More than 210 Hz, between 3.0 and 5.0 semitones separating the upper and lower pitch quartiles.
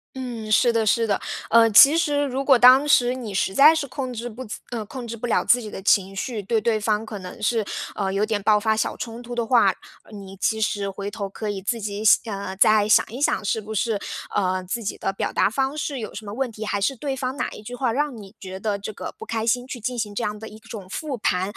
Yes: high, 220 Hz; average, 3.3 semitones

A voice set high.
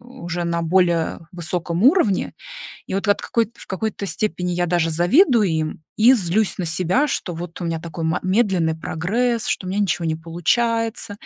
No: medium, 180 Hz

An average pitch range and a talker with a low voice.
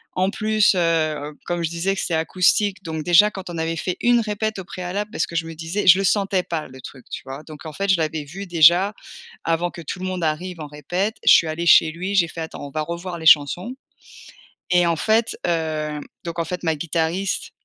No: average, 3.0 semitones; medium, 170 Hz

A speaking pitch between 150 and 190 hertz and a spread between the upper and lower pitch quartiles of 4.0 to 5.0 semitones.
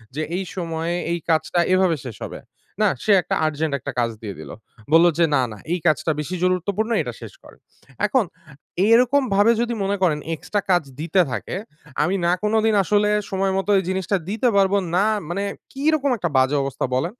Yes: medium, 185 Hz; average, 4.5 semitones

